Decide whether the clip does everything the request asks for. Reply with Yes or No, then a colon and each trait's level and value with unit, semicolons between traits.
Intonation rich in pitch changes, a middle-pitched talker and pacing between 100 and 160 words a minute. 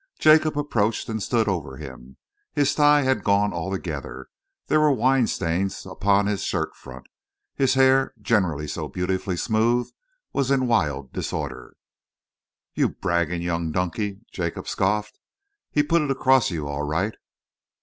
No: wide, 7.4 semitones; low, 100 Hz; average, 140 wpm